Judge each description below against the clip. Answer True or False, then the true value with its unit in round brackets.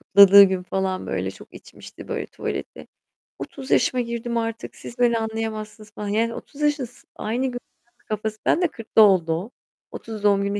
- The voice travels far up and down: False (2.8 semitones)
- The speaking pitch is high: True (220 Hz)